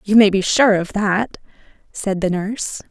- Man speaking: No, female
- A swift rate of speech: No, average, 185 wpm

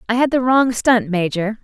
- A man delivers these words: No, female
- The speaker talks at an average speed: No, fast, 220 wpm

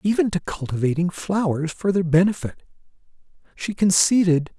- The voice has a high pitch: No, medium, 180 Hz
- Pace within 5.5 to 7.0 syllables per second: No, 5.0 syllables/s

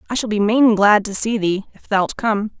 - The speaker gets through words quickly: Yes, fast, 255 wpm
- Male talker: No, female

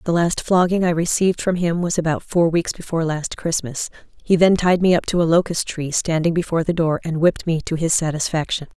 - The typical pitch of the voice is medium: Yes, medium, 170 Hz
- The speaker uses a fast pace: Yes, fast, 225 wpm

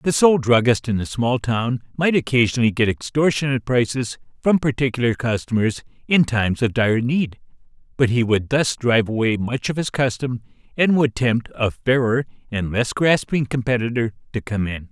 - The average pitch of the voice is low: Yes, low, 120 Hz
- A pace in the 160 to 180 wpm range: Yes, average, 170 wpm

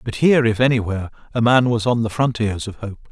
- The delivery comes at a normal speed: No, fast, 230 wpm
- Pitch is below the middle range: Yes, low, 115 Hz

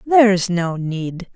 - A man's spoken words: No, female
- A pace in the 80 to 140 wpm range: Yes, slow, 135 wpm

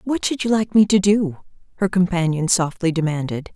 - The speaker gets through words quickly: No, average, 185 wpm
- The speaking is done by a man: No, female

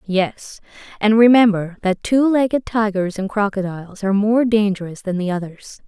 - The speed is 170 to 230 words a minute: No, average, 155 wpm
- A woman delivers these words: Yes, female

